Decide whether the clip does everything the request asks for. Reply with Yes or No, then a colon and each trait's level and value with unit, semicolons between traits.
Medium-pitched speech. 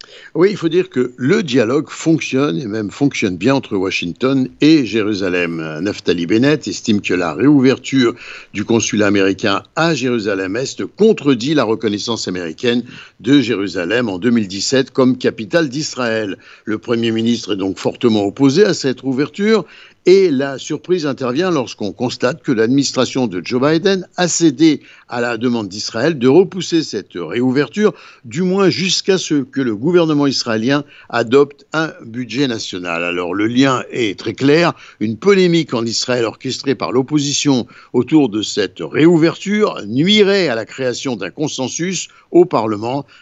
No: low, 130 Hz